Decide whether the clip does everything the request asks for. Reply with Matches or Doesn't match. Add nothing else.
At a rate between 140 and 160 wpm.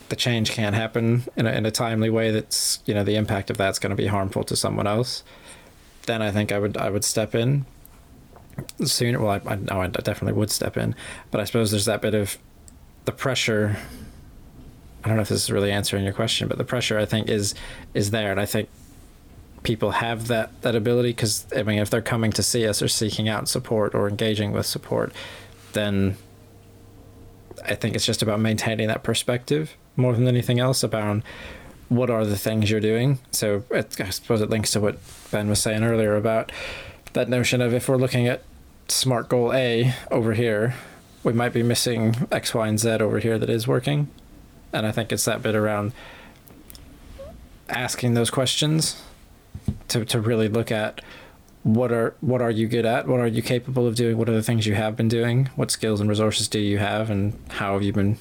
Doesn't match